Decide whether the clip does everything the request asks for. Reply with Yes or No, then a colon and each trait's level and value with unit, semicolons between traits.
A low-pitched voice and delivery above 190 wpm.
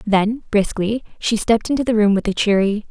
No: high, 215 Hz; fast, 205 wpm